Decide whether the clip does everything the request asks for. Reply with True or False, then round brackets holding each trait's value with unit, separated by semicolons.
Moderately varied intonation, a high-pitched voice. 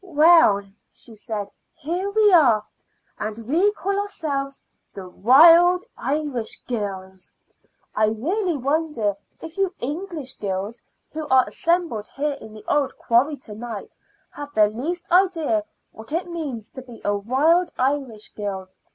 False (7.4 semitones; 275 Hz)